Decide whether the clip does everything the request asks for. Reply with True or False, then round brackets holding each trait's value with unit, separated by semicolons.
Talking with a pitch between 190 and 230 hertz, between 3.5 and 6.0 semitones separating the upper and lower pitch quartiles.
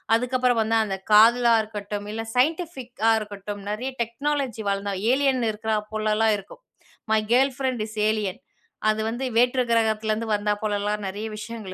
False (220 Hz; 2.9 semitones)